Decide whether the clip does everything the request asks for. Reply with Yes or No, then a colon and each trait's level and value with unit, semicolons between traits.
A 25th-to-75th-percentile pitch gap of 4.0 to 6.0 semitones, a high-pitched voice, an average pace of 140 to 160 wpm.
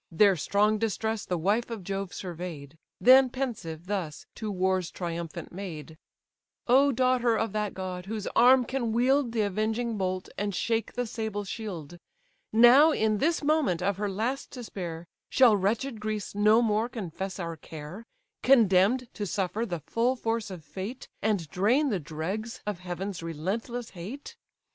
Yes: average, 4.4 semitones; high, 210 Hz; average, 155 wpm